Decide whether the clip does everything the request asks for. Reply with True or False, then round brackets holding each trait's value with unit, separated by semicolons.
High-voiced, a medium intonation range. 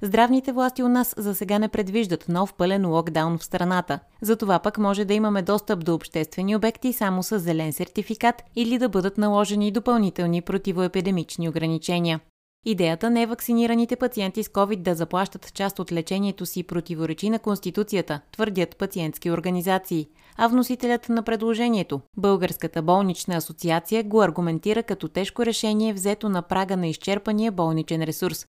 True (195 Hz; 4.1 semitones)